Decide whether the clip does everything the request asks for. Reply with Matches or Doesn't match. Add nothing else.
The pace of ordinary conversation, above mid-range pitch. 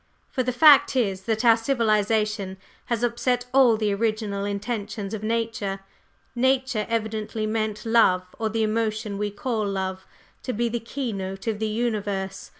Matches